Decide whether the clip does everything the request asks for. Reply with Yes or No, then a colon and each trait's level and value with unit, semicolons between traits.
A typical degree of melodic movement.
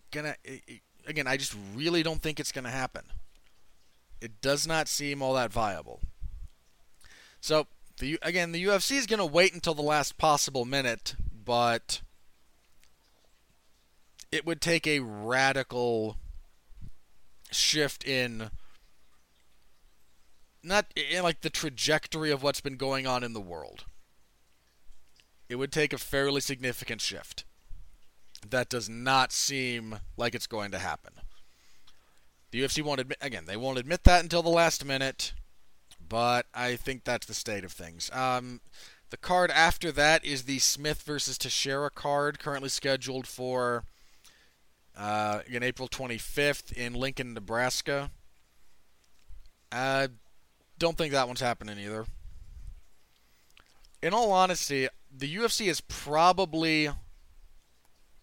No: wide, 5.8 semitones